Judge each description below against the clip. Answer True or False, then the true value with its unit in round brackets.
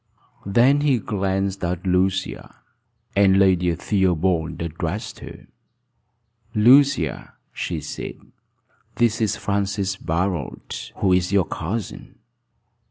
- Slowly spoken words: True (100 wpm)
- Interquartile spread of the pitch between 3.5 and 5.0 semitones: False (2.7 semitones)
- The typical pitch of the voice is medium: False (95 Hz)